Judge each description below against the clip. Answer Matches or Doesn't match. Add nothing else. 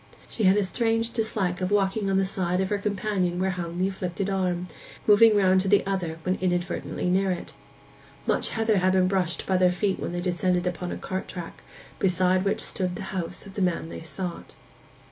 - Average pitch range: Doesn't match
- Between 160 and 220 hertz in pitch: Matches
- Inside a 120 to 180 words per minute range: Doesn't match